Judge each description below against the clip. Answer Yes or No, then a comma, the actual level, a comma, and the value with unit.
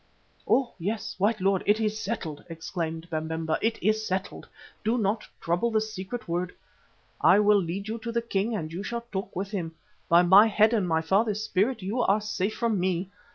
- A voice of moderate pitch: No, high, 200 Hz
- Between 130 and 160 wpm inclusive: No, average, 195 wpm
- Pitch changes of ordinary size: Yes, average, 3.7 semitones